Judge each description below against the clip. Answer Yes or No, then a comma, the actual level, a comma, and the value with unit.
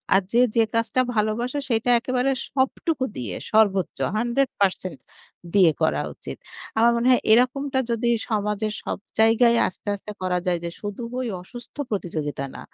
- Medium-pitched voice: No, high, 225 Hz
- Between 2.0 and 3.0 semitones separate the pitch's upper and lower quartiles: No, average, 3.9 semitones